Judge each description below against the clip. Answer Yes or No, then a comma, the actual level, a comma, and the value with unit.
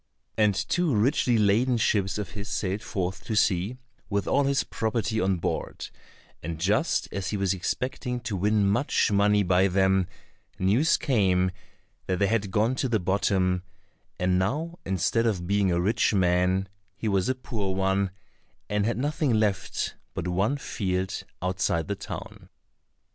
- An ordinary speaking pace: Yes, average, 160 wpm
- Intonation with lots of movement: No, average, 3.3 semitones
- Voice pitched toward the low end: Yes, low, 100 Hz